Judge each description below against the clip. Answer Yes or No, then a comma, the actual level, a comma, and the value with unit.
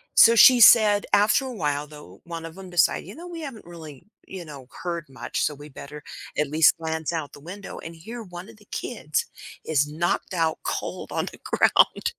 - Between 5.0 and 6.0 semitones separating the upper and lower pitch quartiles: Yes, wide, 5.5 semitones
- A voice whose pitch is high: No, medium, 170 Hz